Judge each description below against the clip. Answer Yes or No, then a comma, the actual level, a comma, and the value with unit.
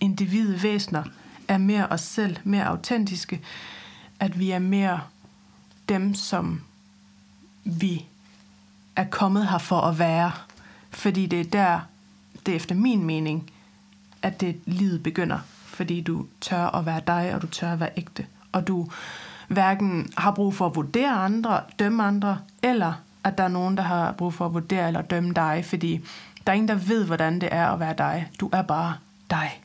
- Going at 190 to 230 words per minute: No, average, 175 wpm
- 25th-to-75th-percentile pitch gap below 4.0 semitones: Yes, average, 2.9 semitones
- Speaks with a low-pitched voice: No, medium, 180 Hz